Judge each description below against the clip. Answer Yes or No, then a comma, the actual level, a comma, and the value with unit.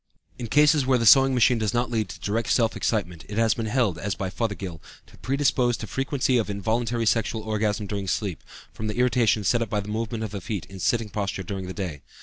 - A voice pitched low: Yes, low, 110 Hz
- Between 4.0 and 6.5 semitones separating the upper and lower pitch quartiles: No, average, 3.0 semitones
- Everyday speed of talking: No, fast, 235 wpm